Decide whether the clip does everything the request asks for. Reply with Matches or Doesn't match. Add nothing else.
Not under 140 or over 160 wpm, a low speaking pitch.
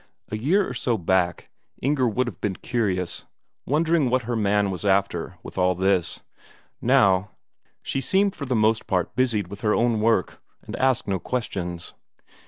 Doesn't match